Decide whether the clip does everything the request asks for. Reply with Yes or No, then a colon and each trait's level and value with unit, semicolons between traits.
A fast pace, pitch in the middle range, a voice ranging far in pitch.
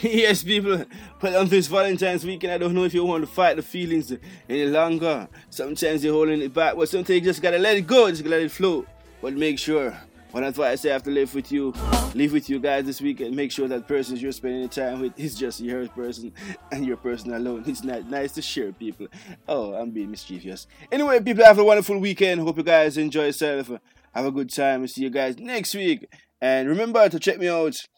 Yes: fast, 230 wpm; medium, 155 Hz; wide, 5.8 semitones